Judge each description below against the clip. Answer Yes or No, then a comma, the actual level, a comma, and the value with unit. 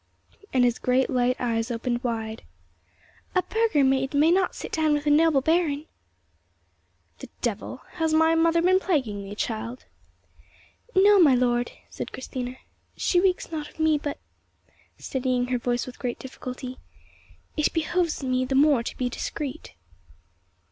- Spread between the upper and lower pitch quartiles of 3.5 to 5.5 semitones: Yes, average, 4.5 semitones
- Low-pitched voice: No, very high, 265 Hz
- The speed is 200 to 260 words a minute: No, average, 145 wpm